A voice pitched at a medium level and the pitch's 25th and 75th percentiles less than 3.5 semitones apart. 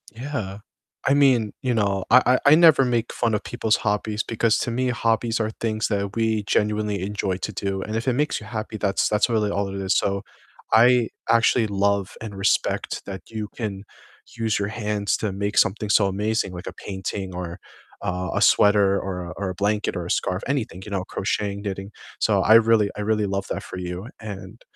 No: low, 105 Hz; narrow, 2.5 semitones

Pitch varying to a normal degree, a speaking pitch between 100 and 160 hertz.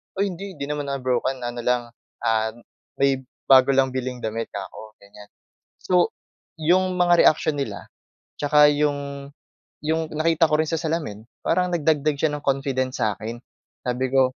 Yes: average, 4.1 semitones; medium, 140 Hz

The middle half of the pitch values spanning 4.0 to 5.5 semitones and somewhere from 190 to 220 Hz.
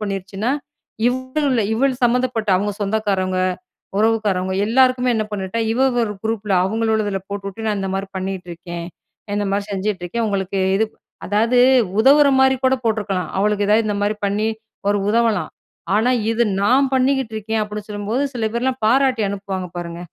No: average, 3.3 semitones; high, 215 Hz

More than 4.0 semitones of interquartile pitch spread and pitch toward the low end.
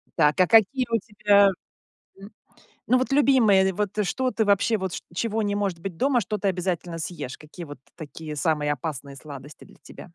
No: wide, 5.4 semitones; high, 190 Hz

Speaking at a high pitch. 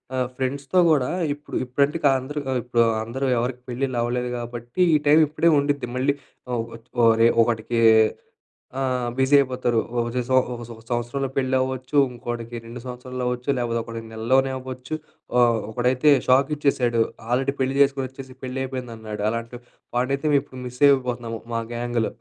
No: low, 125 Hz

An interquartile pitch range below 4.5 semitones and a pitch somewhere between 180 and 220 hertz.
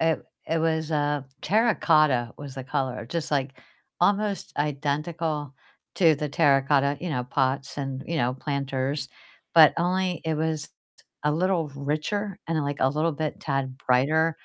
No: average, 2.9 semitones; medium, 150 Hz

